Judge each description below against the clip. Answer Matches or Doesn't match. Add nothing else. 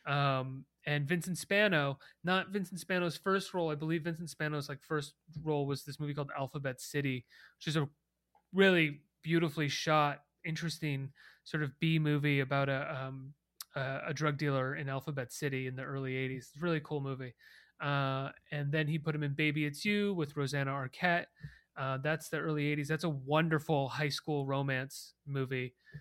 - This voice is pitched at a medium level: Matches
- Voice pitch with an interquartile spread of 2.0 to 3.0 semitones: Matches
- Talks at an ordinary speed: Matches